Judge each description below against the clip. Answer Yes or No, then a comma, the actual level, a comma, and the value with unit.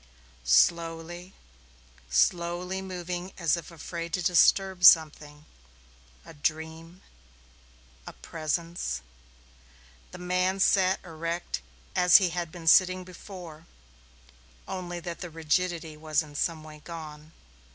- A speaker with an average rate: No, slow, 110 wpm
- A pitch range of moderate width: No, narrow, 2.1 semitones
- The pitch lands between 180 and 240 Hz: No, medium, 170 Hz